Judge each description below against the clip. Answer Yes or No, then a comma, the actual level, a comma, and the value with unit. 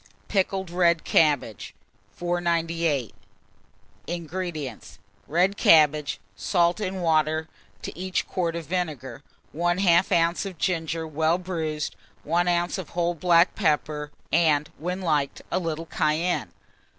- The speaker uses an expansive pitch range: No, narrow, 2.4 semitones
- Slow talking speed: Yes, slow, 115 wpm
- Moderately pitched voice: Yes, medium, 170 Hz